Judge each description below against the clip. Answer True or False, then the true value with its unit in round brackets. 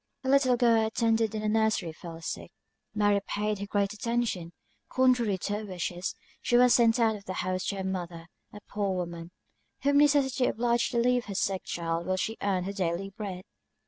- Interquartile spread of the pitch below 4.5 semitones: True (4.1 semitones)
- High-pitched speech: True (210 Hz)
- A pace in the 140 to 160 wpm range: False (200 wpm)